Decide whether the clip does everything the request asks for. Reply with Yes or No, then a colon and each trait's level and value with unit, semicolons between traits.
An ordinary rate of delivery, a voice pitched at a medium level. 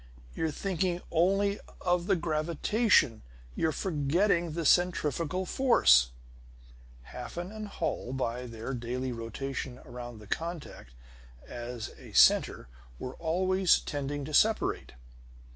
No: slow, 110 wpm; medium, 160 Hz